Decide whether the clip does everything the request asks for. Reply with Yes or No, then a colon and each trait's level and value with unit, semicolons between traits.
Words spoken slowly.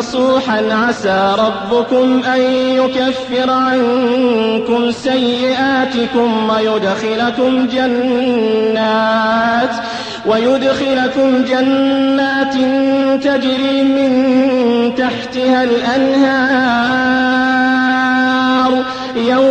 Yes: slow, 50 wpm